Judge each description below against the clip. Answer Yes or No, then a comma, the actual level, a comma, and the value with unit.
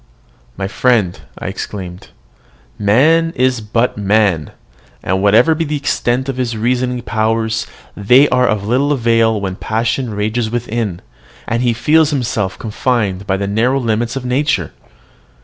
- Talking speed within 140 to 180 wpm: Yes, average, 145 wpm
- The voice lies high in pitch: No, low, 115 Hz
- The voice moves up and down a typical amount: Yes, average, 3.4 semitones